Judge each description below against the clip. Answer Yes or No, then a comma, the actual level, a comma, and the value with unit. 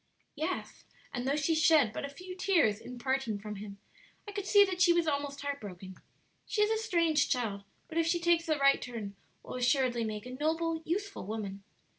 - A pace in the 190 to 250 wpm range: Yes, average, 200 wpm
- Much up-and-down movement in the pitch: Yes, wide, 6.6 semitones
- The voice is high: Yes, very high, 285 Hz